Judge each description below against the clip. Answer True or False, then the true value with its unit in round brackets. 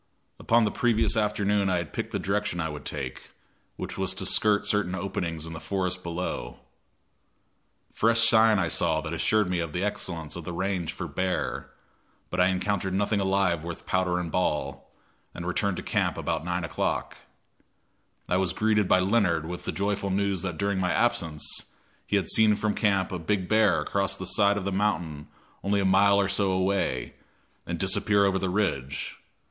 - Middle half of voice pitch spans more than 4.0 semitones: False (2.7 semitones)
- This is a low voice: True (95 Hz)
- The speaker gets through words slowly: False (185 wpm)